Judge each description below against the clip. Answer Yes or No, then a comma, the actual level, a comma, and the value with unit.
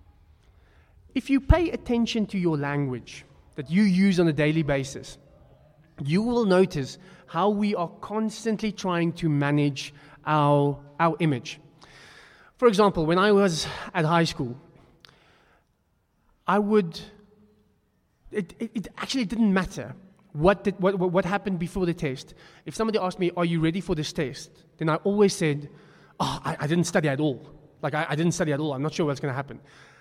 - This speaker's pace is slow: No, average, 170 wpm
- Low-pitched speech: No, medium, 165 Hz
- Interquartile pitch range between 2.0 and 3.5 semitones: No, average, 5.1 semitones